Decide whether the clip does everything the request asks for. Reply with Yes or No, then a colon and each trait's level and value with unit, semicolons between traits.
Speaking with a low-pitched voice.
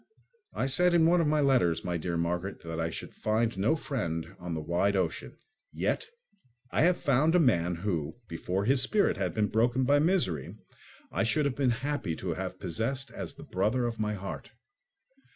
Yes: low, 110 Hz